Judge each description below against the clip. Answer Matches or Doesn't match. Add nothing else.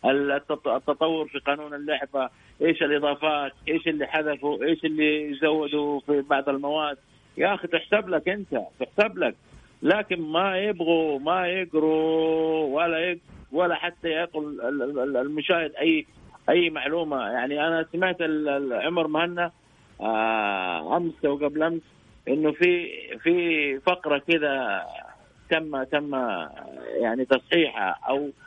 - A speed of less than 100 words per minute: Doesn't match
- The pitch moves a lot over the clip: Doesn't match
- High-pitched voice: Doesn't match